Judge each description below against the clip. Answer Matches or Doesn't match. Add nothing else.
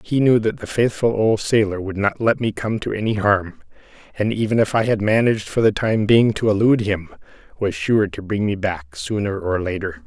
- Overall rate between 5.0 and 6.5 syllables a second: Matches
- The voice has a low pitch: Matches